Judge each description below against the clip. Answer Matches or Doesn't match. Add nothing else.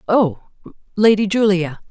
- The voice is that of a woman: Matches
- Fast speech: Doesn't match